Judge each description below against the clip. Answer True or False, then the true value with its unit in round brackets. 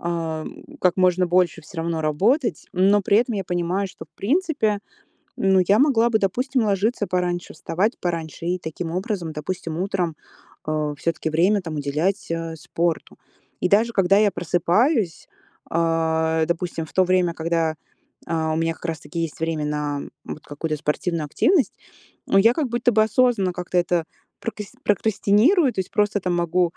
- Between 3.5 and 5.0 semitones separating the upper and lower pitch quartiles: True (4.1 semitones)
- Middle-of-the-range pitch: True (180 Hz)